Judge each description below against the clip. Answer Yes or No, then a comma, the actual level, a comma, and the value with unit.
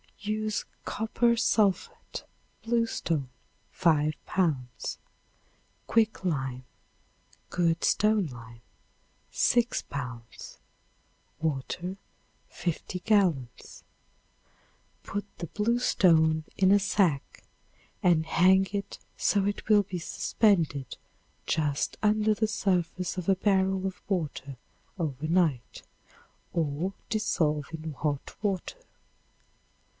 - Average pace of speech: No, slow, 90 wpm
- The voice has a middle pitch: Yes, medium, 180 Hz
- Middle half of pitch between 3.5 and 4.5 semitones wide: No, average, 5.2 semitones